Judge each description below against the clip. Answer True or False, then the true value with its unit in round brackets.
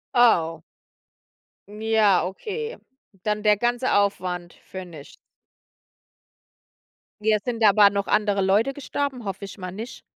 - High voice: True (210 Hz)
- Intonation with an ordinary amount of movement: True (3.4 semitones)